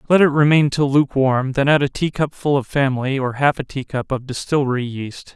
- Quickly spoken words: Yes, fast, 235 wpm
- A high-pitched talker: No, low, 135 Hz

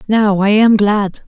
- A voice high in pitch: Yes, high, 205 Hz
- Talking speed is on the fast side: No, average, 190 wpm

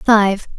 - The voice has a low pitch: No, high, 210 Hz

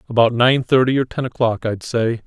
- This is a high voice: No, low, 120 Hz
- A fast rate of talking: Yes, fast, 210 wpm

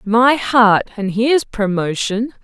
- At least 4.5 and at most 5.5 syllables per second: No, 3.8 syllables/s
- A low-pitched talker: No, high, 225 Hz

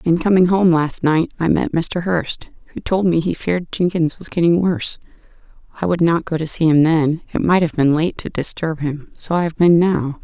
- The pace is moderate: No, fast, 230 wpm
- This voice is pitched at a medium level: Yes, medium, 165 Hz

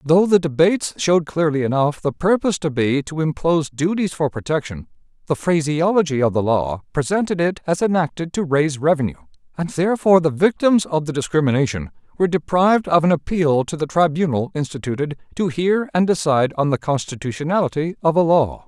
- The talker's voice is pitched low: No, medium, 155 Hz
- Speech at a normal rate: Yes, average, 170 wpm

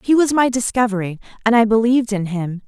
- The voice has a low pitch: No, high, 225 Hz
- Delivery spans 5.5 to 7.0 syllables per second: Yes, 6.1 syllables/s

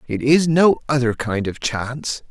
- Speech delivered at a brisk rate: No, average, 180 wpm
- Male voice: Yes, male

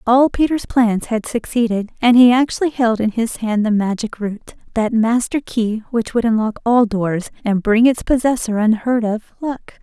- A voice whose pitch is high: Yes, high, 230 Hz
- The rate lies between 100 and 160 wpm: No, average, 175 wpm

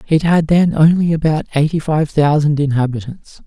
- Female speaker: No, male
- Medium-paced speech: Yes, average, 155 wpm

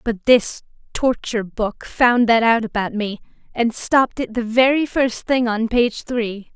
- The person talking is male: No, female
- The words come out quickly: No, average, 175 wpm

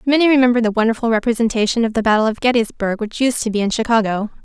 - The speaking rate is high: Yes, fast, 215 wpm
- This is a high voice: Yes, high, 230 Hz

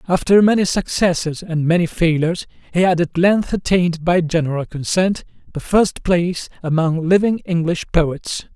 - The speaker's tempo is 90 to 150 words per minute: Yes, average, 145 wpm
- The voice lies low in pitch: No, medium, 175 Hz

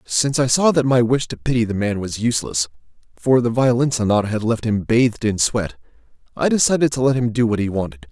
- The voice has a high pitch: No, low, 115 Hz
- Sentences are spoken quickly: Yes, fast, 230 wpm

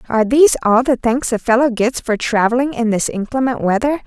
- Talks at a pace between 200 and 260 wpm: Yes, fast, 205 wpm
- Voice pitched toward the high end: Yes, high, 240 Hz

